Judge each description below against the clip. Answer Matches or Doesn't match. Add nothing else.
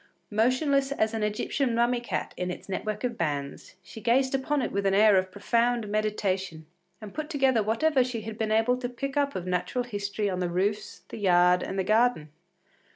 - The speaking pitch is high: Matches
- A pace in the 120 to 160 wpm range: Doesn't match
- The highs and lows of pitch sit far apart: Doesn't match